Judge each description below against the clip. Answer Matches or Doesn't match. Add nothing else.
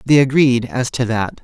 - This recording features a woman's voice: Doesn't match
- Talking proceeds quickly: Matches